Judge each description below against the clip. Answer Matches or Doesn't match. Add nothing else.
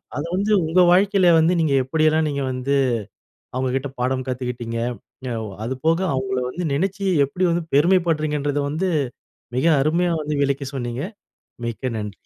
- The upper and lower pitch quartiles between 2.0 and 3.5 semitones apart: Doesn't match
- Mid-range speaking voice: Matches